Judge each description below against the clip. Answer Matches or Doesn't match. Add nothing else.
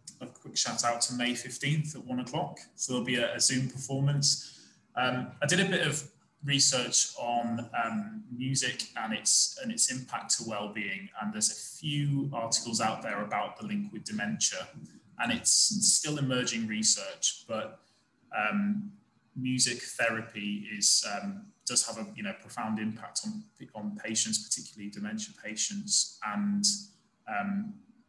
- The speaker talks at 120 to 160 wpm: Matches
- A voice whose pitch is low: Doesn't match